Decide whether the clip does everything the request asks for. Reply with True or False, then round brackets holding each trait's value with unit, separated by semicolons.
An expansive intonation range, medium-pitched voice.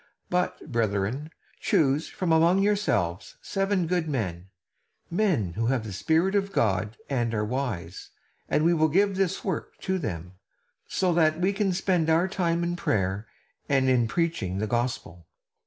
True (8.7 semitones; 155 Hz)